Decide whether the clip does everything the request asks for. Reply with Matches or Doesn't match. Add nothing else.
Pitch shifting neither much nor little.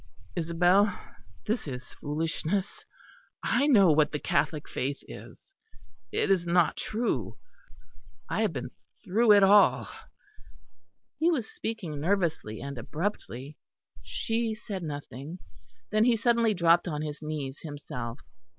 Doesn't match